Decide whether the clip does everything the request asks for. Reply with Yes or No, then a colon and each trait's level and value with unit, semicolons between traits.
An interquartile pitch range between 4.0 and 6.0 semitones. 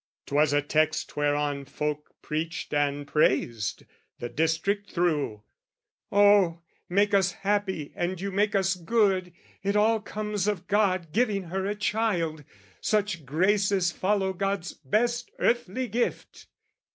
Yes: average, 4.7 semitones